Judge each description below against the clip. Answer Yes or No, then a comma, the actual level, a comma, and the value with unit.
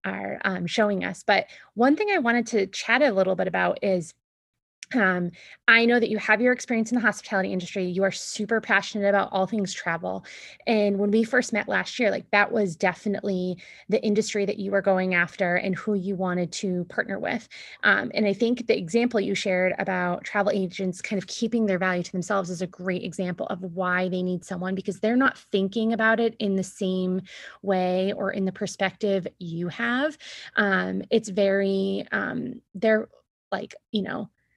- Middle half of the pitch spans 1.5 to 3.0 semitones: Yes, average, 2.7 semitones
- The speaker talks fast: No, average, 195 wpm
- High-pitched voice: Yes, high, 195 Hz